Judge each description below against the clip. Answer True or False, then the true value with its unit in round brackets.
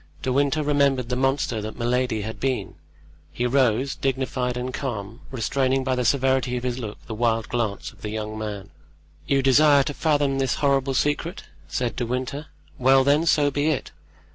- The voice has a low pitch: True (130 Hz)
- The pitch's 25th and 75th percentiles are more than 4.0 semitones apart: False (2.7 semitones)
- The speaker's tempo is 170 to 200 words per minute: True (180 wpm)